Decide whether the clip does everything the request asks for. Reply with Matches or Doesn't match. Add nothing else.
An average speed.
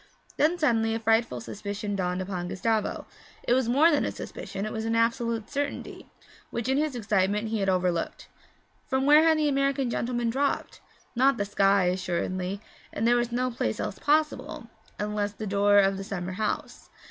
Matches